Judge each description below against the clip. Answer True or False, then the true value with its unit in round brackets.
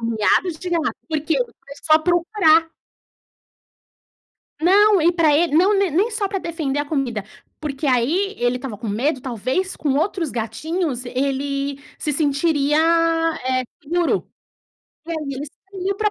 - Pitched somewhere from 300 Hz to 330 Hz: True (310 Hz)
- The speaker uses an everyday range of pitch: True (4.6 semitones)